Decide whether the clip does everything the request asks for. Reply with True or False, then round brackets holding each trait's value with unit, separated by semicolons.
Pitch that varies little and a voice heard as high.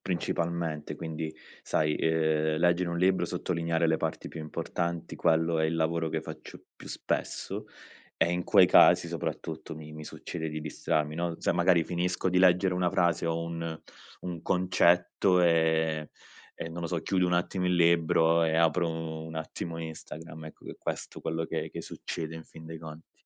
False (1.4 semitones; 80 Hz)